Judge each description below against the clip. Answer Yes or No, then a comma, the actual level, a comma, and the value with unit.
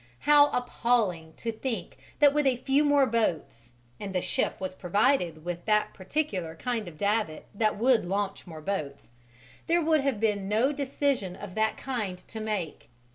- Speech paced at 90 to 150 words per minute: No, average, 170 wpm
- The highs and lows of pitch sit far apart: Yes, wide, 6.3 semitones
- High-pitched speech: Yes, high, 215 Hz